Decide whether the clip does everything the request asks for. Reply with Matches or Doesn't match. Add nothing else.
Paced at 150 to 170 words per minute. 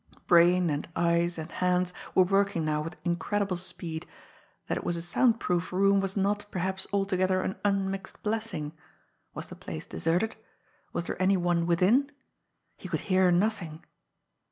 Matches